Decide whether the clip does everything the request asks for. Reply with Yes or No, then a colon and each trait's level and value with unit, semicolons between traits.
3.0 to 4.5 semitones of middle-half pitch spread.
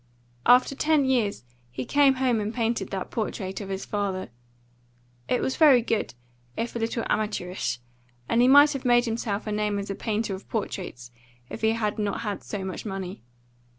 Yes: average, 3.6 semitones